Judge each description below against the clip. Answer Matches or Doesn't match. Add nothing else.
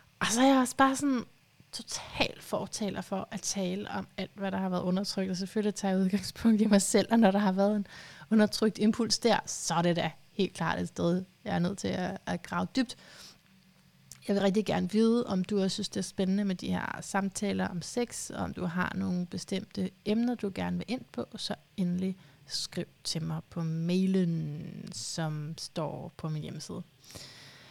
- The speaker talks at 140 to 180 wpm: Doesn't match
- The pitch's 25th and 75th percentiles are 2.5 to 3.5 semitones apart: Matches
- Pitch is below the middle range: Doesn't match